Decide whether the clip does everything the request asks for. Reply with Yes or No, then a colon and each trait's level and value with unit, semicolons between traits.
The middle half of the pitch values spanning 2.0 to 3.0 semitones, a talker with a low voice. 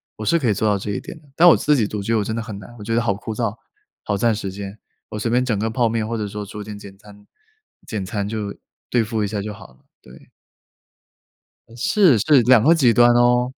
Yes: average, 2.7 semitones; low, 110 Hz